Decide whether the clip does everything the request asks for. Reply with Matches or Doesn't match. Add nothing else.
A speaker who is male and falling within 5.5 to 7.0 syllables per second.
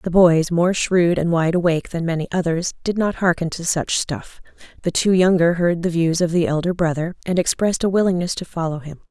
Doesn't match